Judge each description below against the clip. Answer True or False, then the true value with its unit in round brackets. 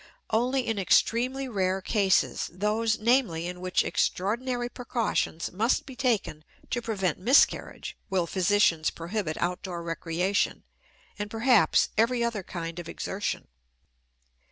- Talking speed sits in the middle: False (120 wpm)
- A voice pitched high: True (205 Hz)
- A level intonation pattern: False (4.8 semitones)